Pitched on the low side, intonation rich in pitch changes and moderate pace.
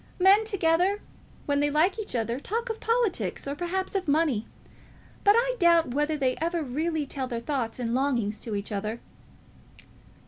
No: very high, 305 Hz; wide, 6.9 semitones; average, 170 wpm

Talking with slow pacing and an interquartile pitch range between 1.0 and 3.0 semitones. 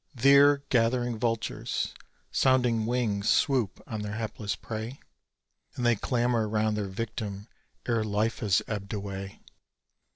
Yes: slow, 125 wpm; narrow, 2.6 semitones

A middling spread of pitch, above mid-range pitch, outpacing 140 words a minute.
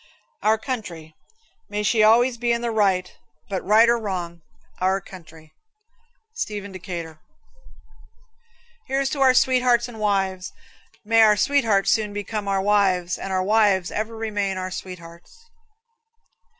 No: average, 3.4 semitones; high, 205 Hz; slow, 135 wpm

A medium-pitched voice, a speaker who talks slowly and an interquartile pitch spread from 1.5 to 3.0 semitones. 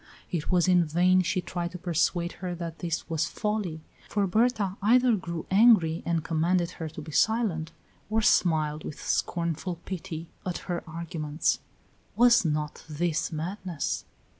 No: medium, 175 Hz; average, 150 wpm; average, 2.7 semitones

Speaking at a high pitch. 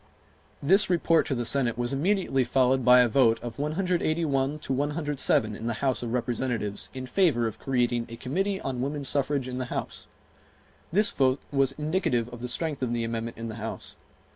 No: low, 130 Hz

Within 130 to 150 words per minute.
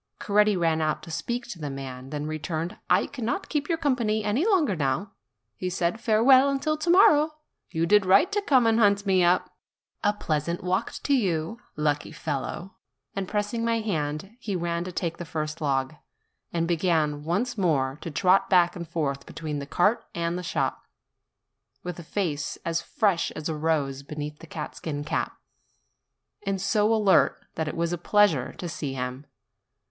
No: average, 180 wpm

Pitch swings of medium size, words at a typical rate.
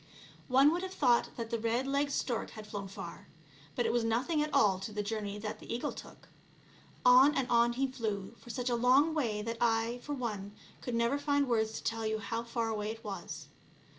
No: average, 3.2 semitones; fast, 220 wpm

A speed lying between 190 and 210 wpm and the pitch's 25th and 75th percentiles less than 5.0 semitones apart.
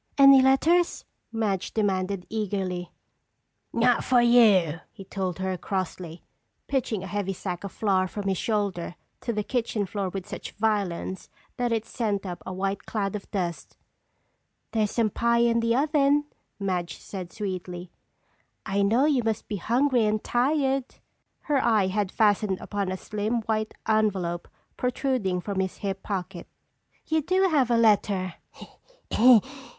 No: average, 145 wpm; average, 3.8 semitones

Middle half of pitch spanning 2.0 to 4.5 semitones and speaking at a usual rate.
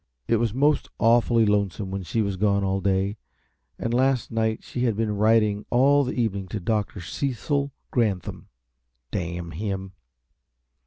Yes: average, 3.3 semitones; average, 150 wpm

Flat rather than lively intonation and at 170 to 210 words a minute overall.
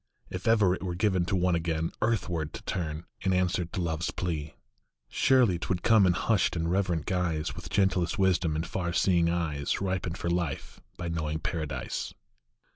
Yes: narrow, 2.3 semitones; average, 185 wpm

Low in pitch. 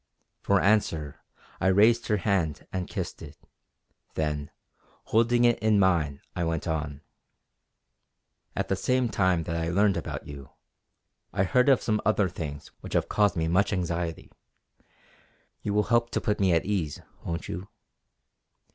Yes: very low, 95 Hz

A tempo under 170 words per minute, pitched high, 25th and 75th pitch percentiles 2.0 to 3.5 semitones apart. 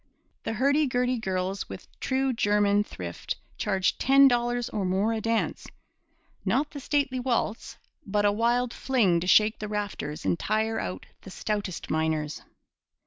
No: average, 150 wpm; high, 215 Hz; average, 4.4 semitones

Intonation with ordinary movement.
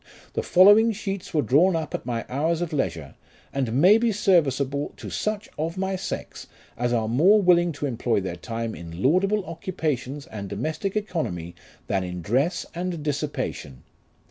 No: wide, 7.5 semitones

